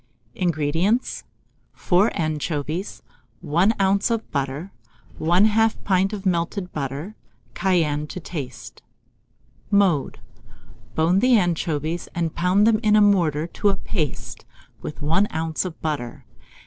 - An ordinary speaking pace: No, slow, 120 wpm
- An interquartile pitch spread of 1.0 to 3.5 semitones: No, average, 4.4 semitones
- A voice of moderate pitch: Yes, medium, 175 Hz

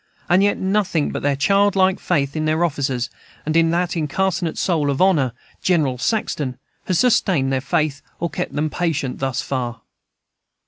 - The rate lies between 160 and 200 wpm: Yes, average, 165 wpm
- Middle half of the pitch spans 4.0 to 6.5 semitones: Yes, average, 4.9 semitones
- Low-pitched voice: No, medium, 155 Hz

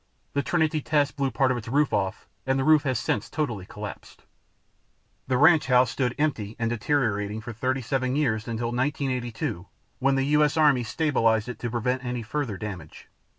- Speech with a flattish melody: No, average, 3.9 semitones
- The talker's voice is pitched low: Yes, low, 125 Hz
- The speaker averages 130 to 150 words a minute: No, average, 175 wpm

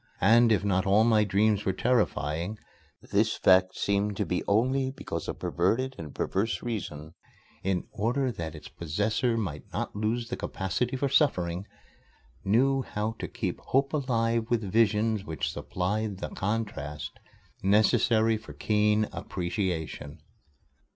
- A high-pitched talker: No, low, 105 Hz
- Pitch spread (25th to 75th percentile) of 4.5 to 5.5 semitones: No, average, 3.6 semitones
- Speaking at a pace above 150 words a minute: No, slow, 135 wpm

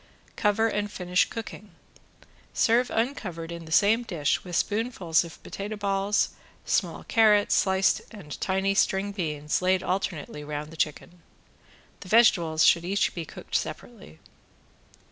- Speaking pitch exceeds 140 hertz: Yes, high, 190 Hz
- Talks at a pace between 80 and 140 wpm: Yes, slow, 135 wpm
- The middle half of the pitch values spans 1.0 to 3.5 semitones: No, average, 4.0 semitones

